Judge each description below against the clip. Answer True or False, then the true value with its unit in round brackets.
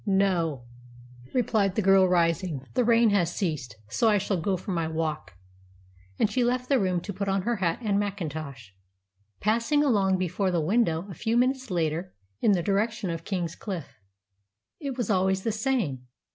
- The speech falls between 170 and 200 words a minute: True (175 wpm)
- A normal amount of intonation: True (4.7 semitones)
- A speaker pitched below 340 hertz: True (190 Hz)